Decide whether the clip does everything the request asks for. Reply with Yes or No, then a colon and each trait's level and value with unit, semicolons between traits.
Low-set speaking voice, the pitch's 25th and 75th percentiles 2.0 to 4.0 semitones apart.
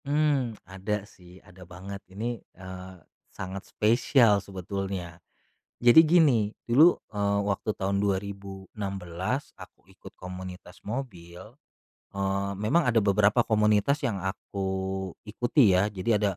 Yes: low, 100 Hz; average, 3.1 semitones